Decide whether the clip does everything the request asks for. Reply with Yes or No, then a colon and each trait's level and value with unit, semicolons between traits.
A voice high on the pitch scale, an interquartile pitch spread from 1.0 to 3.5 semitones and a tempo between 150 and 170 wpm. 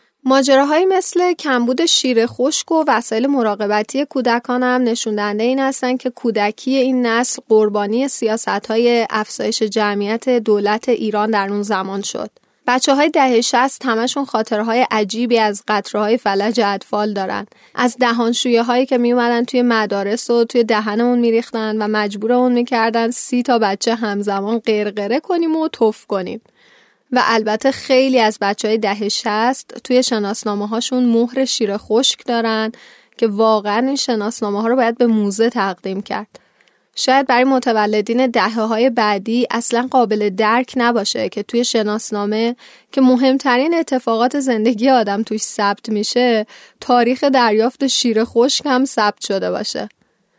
No: high, 235 Hz; average, 2.8 semitones; average, 140 wpm